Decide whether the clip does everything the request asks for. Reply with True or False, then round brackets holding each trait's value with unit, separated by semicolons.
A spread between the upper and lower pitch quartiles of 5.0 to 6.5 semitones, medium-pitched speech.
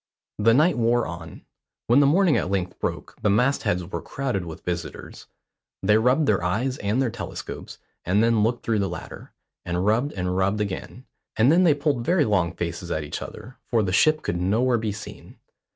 False (5.5 semitones; 110 Hz)